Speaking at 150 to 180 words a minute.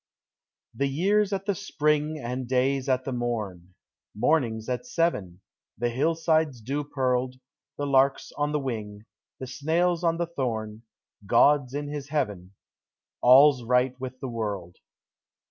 No: average, 140 wpm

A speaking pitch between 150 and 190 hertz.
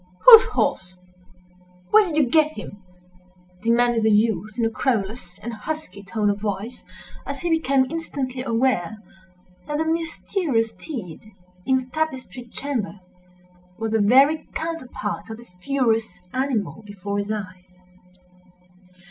No: high, 235 Hz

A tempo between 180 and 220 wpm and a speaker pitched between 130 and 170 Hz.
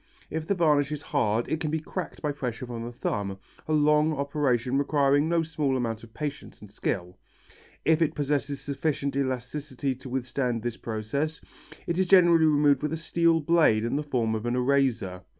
Yes: average, 185 wpm; medium, 140 Hz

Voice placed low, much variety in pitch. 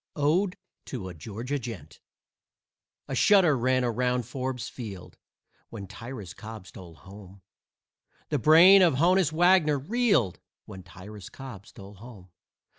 Yes: low, 125 Hz; wide, 7.3 semitones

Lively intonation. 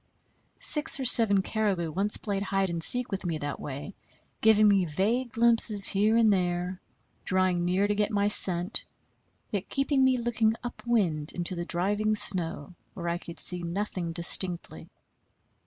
No: average, 3.8 semitones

